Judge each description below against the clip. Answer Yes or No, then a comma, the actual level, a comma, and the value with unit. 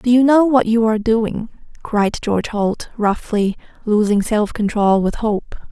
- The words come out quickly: No, average, 170 wpm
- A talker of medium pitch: No, high, 220 Hz